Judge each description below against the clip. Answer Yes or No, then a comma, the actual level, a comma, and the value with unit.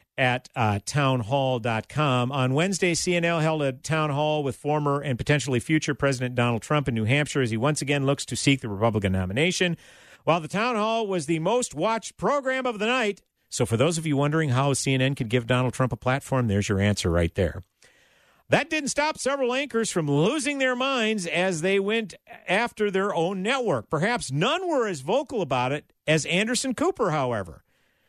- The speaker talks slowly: No, average, 190 wpm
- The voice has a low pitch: No, medium, 150 Hz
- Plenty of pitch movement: Yes, wide, 7.6 semitones